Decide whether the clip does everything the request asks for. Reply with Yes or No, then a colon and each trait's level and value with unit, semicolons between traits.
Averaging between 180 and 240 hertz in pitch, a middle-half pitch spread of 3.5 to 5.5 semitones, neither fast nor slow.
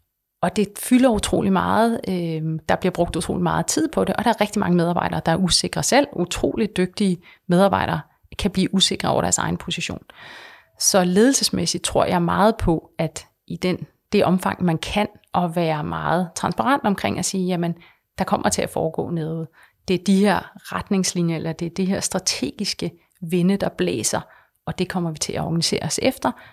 No: medium, 185 Hz; average, 3.1 semitones; average, 190 wpm